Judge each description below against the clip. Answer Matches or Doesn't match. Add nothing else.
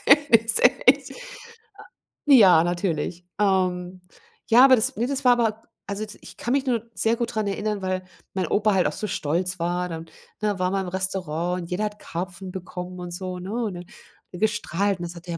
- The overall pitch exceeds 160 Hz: Matches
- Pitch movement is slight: Doesn't match